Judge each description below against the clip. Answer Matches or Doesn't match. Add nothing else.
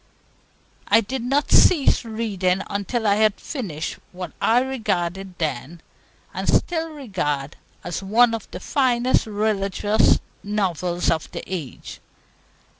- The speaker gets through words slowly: Matches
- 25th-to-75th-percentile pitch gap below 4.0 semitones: Doesn't match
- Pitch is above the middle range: Matches